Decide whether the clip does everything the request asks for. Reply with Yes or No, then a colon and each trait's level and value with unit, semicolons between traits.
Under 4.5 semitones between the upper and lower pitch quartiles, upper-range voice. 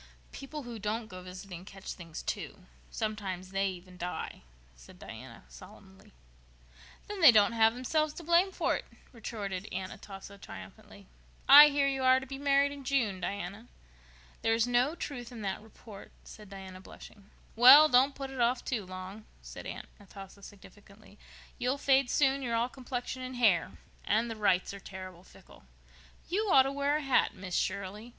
No: wide, 5.5 semitones; high, 220 Hz